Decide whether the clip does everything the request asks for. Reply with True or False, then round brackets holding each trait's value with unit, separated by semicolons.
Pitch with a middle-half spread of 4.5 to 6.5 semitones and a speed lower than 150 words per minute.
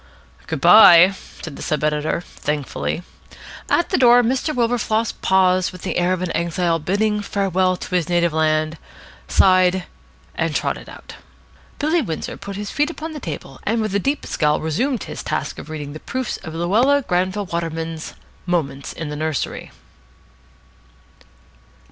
False (5.2 semitones; 155 wpm)